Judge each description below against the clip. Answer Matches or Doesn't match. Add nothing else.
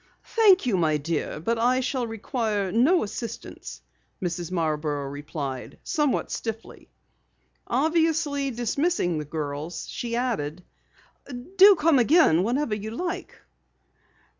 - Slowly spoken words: Matches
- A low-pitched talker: Doesn't match